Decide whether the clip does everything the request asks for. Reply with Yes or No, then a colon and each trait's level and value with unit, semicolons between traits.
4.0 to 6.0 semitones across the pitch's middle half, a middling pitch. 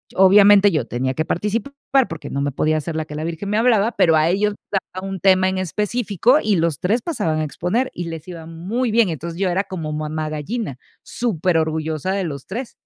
Yes: average, 4.8 semitones; medium, 180 Hz